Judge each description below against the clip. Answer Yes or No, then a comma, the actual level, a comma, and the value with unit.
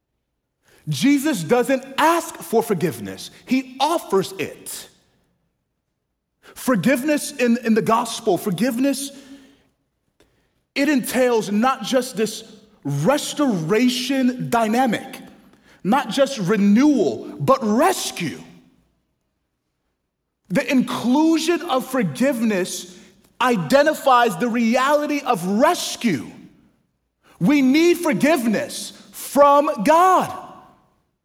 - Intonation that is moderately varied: Yes, average, 4.2 semitones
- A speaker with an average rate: No, slow, 75 wpm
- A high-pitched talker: Yes, very high, 255 Hz